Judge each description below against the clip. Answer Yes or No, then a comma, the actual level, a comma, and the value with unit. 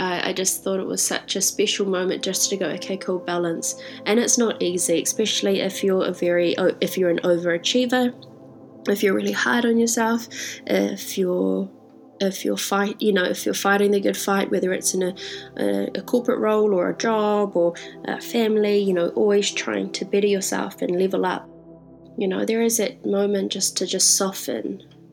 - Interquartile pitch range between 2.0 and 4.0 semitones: Yes, average, 2.9 semitones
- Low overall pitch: No, high, 195 Hz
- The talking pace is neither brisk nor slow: Yes, average, 195 wpm